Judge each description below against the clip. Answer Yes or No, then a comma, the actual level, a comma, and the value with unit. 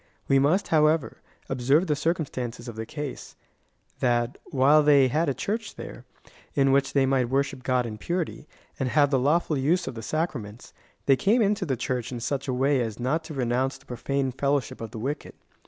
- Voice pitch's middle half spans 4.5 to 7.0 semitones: No, average, 3.4 semitones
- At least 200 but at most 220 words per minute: Yes, fast, 205 wpm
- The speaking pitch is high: No, low, 135 Hz